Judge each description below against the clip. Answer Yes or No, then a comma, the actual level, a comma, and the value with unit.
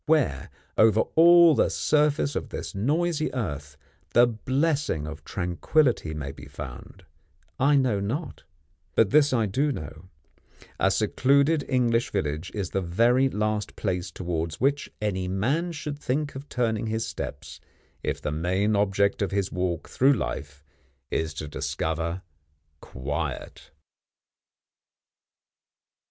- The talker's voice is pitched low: Yes, low, 105 Hz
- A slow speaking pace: Yes, slow, 130 wpm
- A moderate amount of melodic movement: No, wide, 8.3 semitones